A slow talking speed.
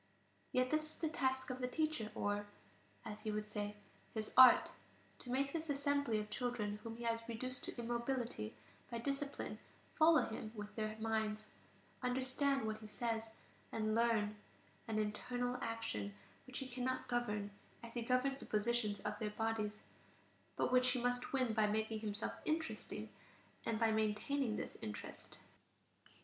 No: average, 160 wpm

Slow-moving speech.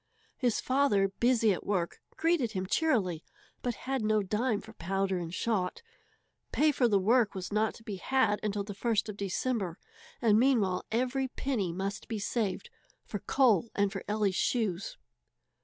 No: average, 165 wpm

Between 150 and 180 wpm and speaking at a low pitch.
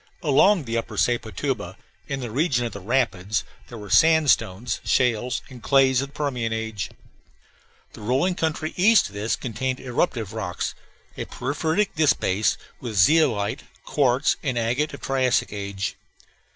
No: average, 140 wpm; low, 125 Hz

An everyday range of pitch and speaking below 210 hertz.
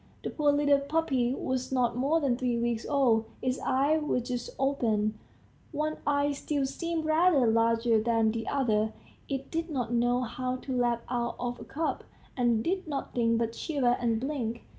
No: average, 3.4 semitones; very high, 255 Hz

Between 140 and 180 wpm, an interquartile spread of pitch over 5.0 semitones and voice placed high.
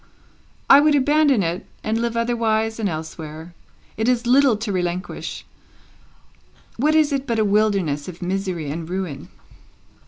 Yes: average, 150 wpm; wide, 5.5 semitones; high, 215 Hz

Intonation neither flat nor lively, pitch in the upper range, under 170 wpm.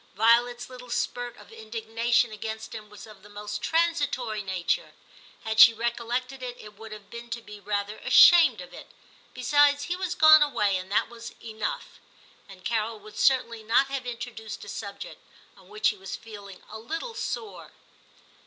No: average, 3.1 semitones; high, 230 Hz; average, 175 wpm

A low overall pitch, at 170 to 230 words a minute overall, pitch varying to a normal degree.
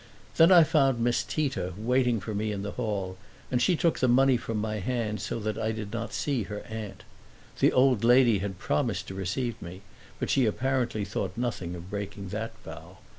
Yes: low, 110 Hz; average, 200 wpm; average, 3.7 semitones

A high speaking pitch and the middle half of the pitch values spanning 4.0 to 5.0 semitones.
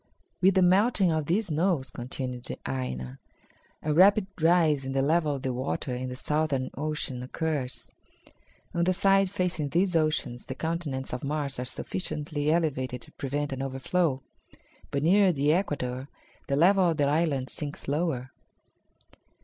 No: medium, 150 Hz; average, 4.5 semitones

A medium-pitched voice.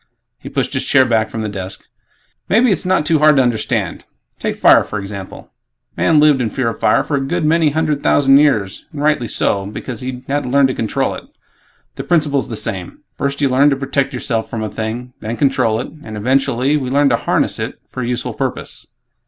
No: low, 130 Hz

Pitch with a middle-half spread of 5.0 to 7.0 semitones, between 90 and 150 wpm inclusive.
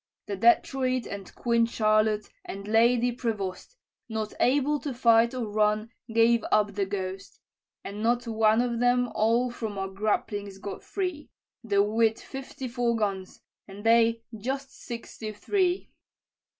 No: average, 2.8 semitones; average, 140 wpm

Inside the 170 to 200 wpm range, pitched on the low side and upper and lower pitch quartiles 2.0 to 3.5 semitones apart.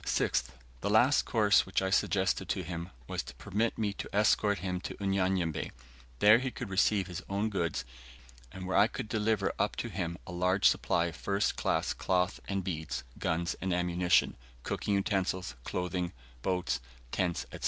Yes: average, 175 wpm; very low, 95 Hz; narrow, 2.5 semitones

